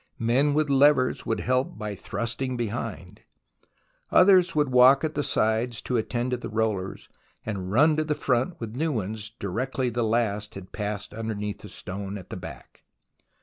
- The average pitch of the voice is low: Yes, low, 115 Hz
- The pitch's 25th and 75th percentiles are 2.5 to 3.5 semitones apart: No, average, 4.0 semitones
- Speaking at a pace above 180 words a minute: No, average, 170 wpm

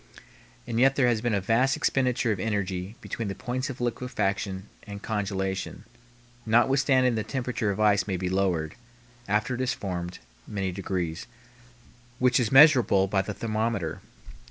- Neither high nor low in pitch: No, low, 105 Hz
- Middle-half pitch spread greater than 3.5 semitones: Yes, average, 4.3 semitones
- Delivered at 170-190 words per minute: No, average, 155 wpm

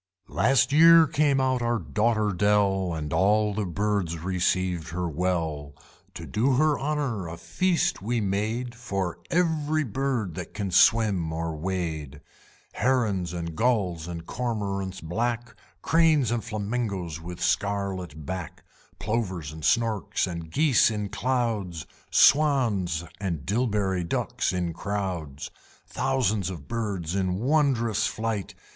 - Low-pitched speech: Yes, low, 100 Hz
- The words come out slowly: Yes, slow, 125 wpm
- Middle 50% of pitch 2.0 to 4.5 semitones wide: No, average, 5.3 semitones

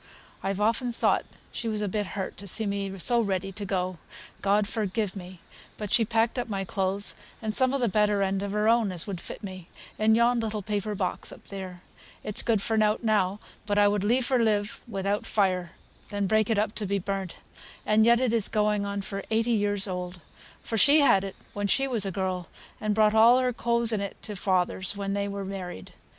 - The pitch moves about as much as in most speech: No, narrow, 2.3 semitones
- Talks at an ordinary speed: No, fast, 215 wpm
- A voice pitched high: Yes, high, 205 Hz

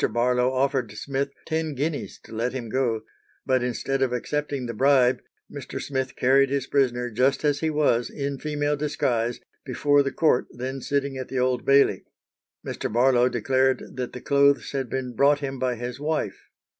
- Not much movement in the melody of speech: Yes, narrow, 2.3 semitones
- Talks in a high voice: No, low, 130 Hz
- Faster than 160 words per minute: Yes, average, 175 wpm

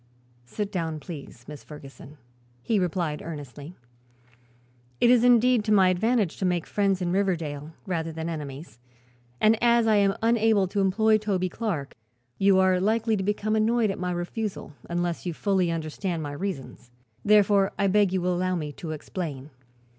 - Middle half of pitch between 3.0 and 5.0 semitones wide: Yes, average, 4.5 semitones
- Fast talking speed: No, average, 165 wpm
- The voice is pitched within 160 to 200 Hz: Yes, medium, 185 Hz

